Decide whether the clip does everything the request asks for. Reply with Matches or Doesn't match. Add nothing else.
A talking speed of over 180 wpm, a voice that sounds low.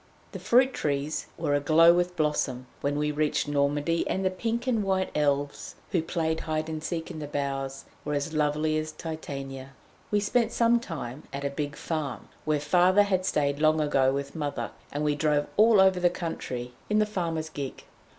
Doesn't match